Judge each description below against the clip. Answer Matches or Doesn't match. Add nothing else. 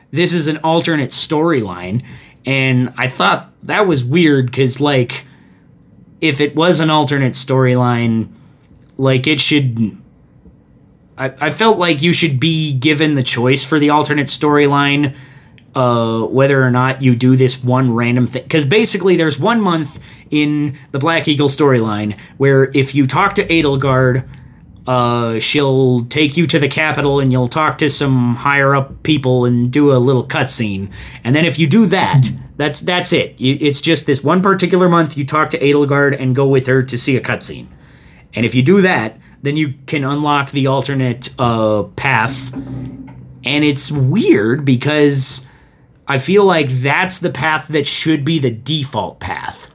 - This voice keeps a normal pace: Matches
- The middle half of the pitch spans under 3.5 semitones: Matches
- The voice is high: Doesn't match